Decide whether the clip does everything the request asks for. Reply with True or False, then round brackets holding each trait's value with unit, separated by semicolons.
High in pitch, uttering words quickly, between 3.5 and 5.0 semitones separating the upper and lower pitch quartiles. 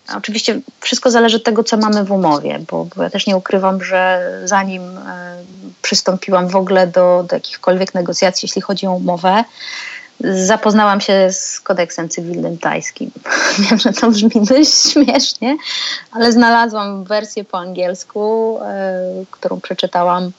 False (200 Hz; 145 wpm; 4.0 semitones)